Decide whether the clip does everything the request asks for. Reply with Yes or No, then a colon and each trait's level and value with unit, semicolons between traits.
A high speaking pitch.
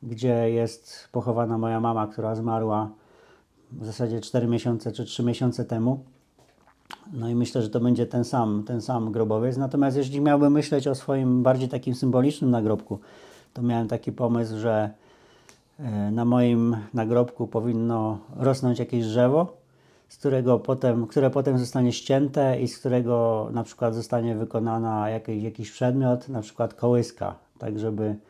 No: low, 120 Hz